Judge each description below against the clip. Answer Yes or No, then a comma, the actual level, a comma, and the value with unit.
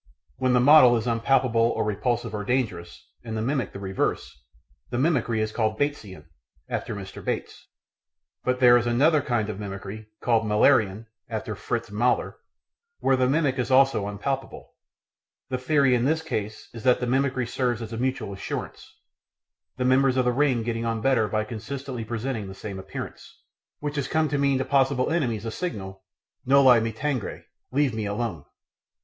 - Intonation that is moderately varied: Yes, average, 3.5 semitones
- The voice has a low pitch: Yes, low, 120 Hz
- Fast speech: No, average, 170 wpm